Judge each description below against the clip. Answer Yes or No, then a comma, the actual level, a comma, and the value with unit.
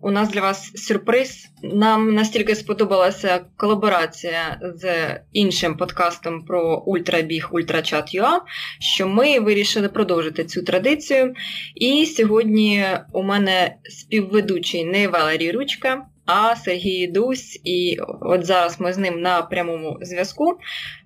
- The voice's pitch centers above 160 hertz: Yes, high, 190 Hz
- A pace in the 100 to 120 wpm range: Yes, average, 115 wpm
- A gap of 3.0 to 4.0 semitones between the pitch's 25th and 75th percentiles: Yes, average, 3.7 semitones